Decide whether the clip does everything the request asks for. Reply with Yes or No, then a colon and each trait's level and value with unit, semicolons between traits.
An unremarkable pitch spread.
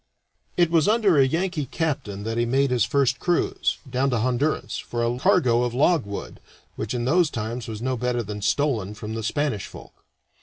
Yes: average, 4.5 semitones